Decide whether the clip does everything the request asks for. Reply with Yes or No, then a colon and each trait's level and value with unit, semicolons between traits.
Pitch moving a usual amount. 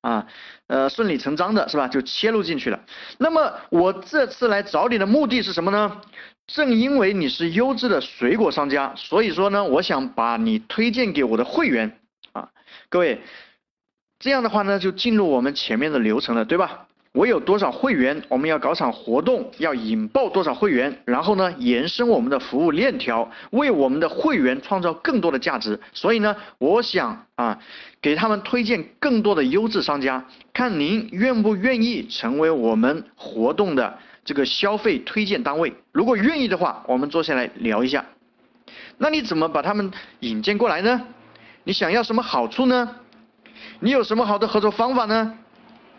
Yes: average, 4.6 semitones